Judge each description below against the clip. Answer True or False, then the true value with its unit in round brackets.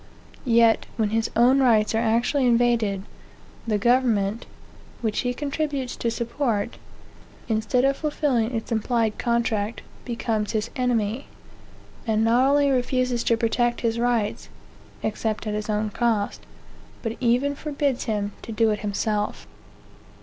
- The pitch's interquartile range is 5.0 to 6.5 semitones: False (2.5 semitones)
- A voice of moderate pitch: False (230 Hz)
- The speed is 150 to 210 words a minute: False (135 wpm)